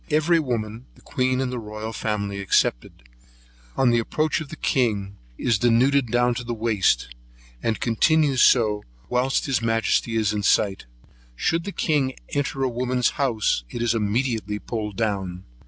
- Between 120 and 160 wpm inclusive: Yes, average, 155 wpm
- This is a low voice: Yes, low, 115 Hz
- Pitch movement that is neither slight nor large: Yes, average, 3.6 semitones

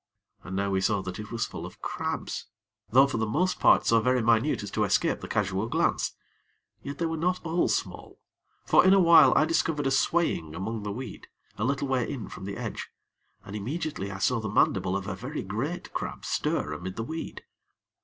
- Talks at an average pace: No, fast, 210 wpm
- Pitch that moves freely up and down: Yes, wide, 6.8 semitones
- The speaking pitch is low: Yes, low, 115 Hz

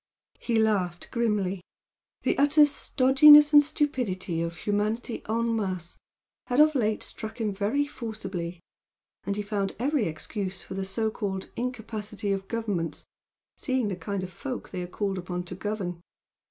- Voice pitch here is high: Yes, high, 210 Hz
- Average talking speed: Yes, average, 155 wpm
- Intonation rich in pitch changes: No, average, 4.3 semitones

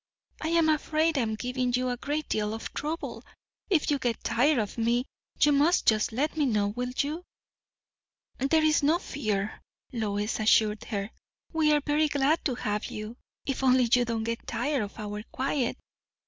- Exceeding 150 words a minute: Yes, average, 185 wpm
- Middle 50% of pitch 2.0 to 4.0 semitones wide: No, average, 5.3 semitones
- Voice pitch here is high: Yes, very high, 250 Hz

